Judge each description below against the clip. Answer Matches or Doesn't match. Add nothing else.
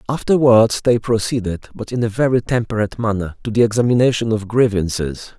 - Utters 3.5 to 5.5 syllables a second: Doesn't match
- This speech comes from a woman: Doesn't match